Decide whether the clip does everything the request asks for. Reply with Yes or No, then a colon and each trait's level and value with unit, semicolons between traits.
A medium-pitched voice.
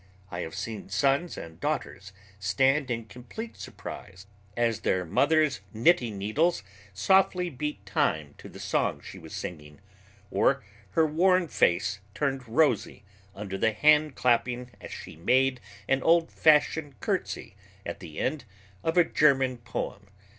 No: low, 125 Hz